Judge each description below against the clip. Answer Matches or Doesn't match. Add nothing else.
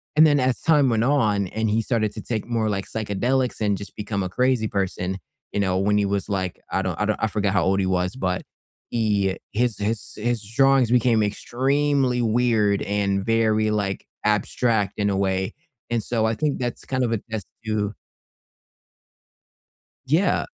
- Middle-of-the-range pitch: Doesn't match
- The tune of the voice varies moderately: Matches